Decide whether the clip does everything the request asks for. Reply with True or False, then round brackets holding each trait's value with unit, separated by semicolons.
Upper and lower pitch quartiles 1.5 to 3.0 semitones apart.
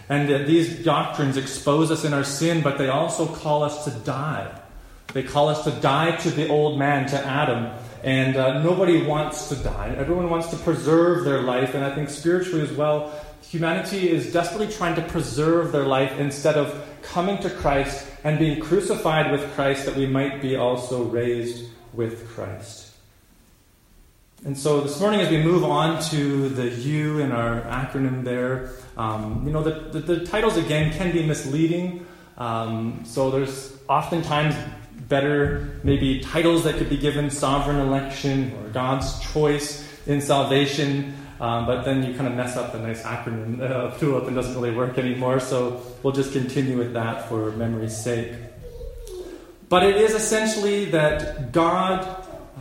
False (3.8 semitones)